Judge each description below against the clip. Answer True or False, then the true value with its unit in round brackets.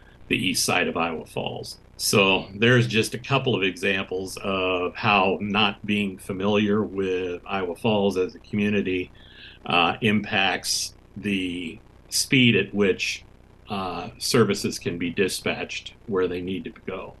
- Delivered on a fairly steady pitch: True (2.3 semitones)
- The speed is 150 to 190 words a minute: False (140 wpm)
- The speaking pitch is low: True (100 Hz)